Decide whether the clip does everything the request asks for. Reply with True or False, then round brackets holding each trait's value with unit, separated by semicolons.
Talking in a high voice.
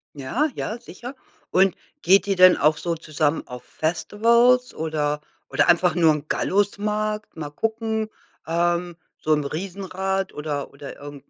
False (175 Hz)